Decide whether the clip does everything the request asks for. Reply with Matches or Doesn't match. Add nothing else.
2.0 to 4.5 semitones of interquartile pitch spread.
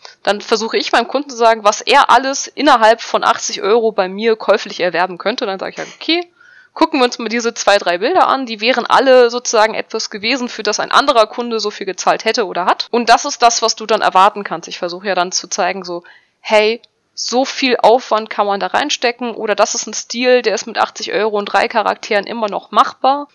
Matches